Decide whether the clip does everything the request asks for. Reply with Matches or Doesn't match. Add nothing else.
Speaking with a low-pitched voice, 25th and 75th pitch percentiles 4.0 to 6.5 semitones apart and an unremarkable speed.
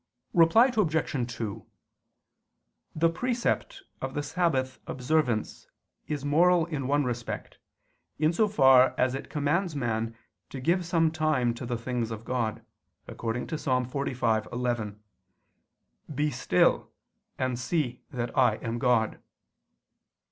Doesn't match